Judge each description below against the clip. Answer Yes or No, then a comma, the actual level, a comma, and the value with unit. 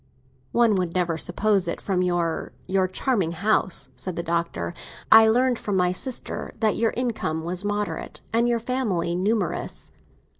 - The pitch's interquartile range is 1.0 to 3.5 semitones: No, average, 4.3 semitones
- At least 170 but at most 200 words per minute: No, average, 150 wpm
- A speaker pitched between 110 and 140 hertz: No, high, 190 Hz